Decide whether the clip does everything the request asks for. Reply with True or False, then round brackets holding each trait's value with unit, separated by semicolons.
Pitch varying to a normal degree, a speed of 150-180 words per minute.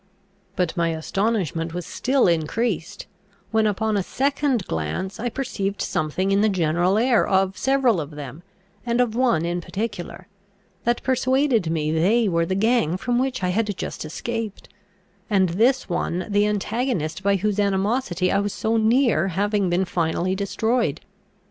True (4.9 semitones; 155 wpm)